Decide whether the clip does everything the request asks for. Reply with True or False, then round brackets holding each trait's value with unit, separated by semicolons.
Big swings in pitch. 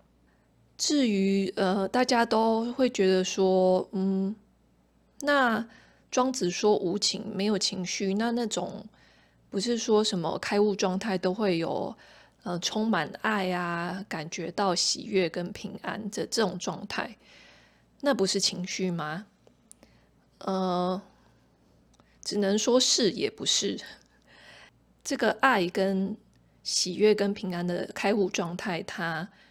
False (2.7 semitones)